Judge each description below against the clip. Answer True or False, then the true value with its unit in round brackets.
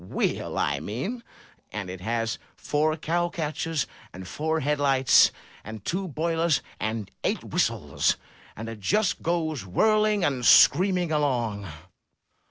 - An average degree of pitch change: False (7.1 semitones)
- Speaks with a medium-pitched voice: True (150 Hz)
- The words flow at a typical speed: False (130 wpm)